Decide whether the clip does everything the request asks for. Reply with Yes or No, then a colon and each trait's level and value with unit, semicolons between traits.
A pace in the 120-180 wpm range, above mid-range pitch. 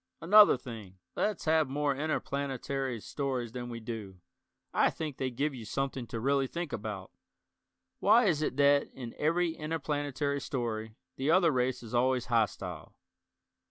No: average, 150 wpm; low, 135 Hz